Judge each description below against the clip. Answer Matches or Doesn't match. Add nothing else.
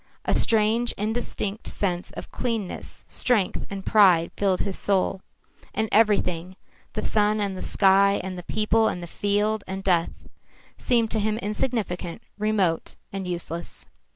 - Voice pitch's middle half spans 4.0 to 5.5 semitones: Doesn't match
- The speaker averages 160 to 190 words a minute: Doesn't match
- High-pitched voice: Matches